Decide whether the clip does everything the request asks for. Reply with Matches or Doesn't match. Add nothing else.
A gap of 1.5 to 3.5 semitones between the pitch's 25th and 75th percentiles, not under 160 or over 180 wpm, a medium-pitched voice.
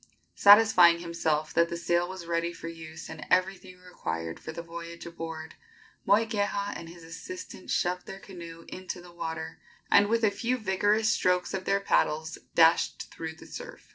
Matches